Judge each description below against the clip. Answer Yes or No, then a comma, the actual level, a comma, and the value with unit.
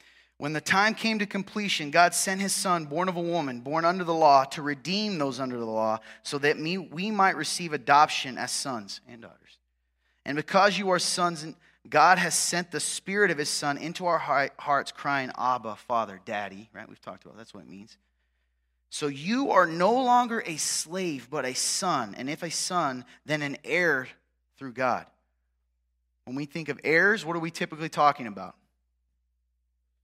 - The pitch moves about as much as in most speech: No, wide, 9.0 semitones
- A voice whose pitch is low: No, medium, 150 Hz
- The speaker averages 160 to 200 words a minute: Yes, average, 185 wpm